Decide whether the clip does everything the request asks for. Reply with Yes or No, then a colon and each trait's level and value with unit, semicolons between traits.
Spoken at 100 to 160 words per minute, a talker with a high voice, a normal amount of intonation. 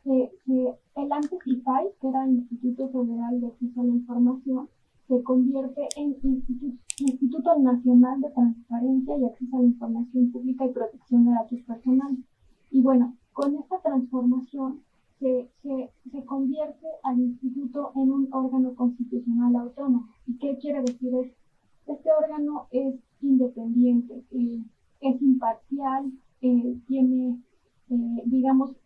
No: average, 135 wpm; very high, 255 Hz; narrow, 1.6 semitones